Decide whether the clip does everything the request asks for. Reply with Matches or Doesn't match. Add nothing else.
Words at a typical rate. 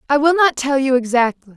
Doesn't match